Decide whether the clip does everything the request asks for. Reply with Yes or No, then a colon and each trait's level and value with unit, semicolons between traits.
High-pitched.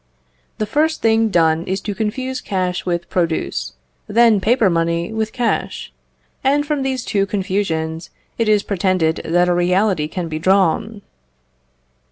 Yes: high, 195 Hz